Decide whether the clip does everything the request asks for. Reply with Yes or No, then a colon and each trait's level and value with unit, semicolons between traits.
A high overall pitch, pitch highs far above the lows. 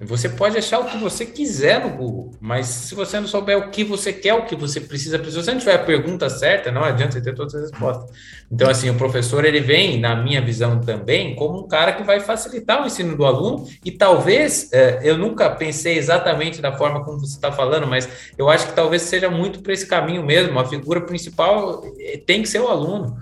No: medium, 155 Hz; wide, 7.2 semitones